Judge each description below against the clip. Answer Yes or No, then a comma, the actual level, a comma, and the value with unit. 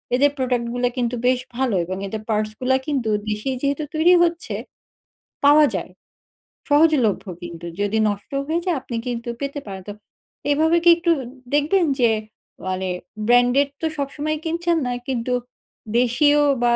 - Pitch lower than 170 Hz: No, very high, 260 Hz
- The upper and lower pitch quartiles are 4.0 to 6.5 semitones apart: Yes, average, 4.5 semitones